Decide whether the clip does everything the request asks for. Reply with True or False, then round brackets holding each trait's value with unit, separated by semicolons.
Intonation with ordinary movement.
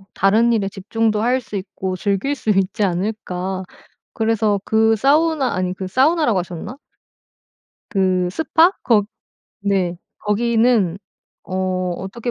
True (3.8 semitones)